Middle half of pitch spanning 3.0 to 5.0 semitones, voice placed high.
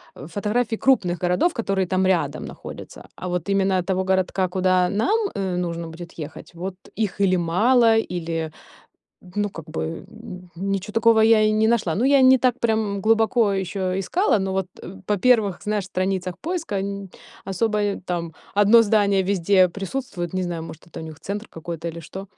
Yes: average, 3.3 semitones; high, 195 Hz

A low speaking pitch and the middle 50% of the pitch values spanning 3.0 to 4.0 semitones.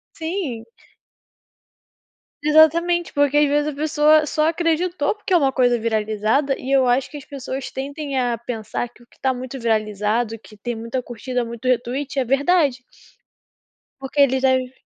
No: very high, 265 Hz; average, 3.7 semitones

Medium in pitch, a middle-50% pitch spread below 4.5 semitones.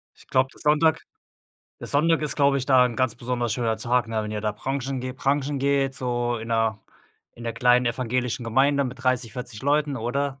No: low, 125 Hz; average, 2.8 semitones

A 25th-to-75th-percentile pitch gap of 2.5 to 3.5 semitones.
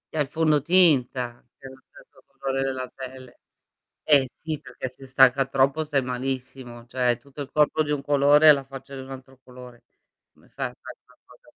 No: narrow, 1.9 semitones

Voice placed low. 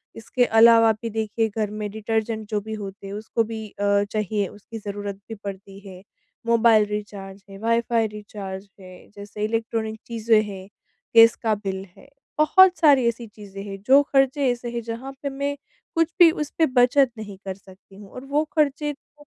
No: high, 220 Hz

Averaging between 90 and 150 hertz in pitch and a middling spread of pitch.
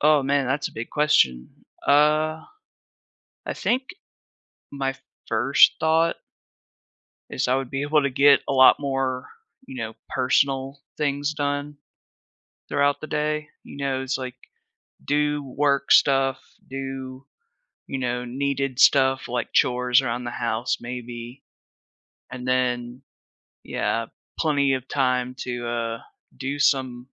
No: low, 135 Hz; narrow, 2.3 semitones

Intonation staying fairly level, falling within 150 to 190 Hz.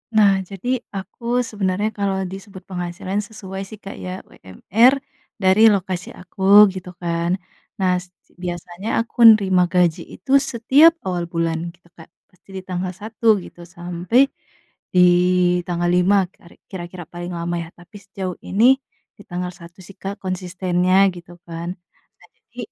Yes: narrow, 2.0 semitones; medium, 185 Hz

